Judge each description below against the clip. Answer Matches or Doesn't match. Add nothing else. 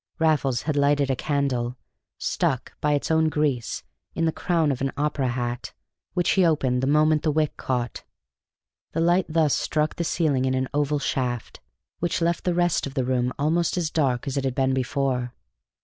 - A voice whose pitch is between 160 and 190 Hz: Doesn't match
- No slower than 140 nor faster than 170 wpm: Doesn't match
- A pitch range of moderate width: Matches